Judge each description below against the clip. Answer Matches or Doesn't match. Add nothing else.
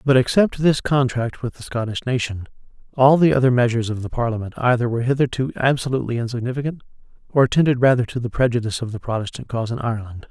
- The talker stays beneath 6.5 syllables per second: Doesn't match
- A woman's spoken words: Doesn't match